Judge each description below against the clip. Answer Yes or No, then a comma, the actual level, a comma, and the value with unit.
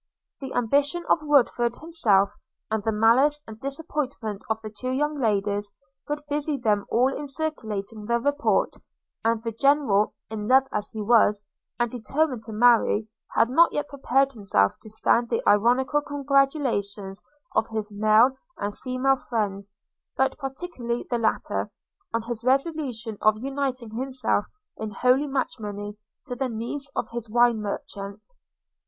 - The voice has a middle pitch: No, high, 240 Hz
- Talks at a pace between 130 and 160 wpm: Yes, average, 150 wpm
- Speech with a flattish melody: No, average, 4.3 semitones